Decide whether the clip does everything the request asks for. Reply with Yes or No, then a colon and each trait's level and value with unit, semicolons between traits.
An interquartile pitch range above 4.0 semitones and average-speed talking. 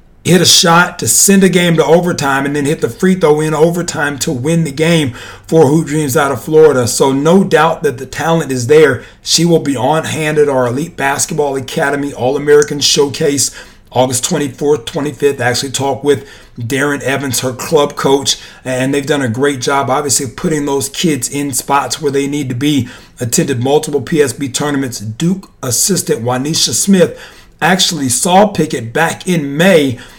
No: average, 3.0 semitones; average, 180 wpm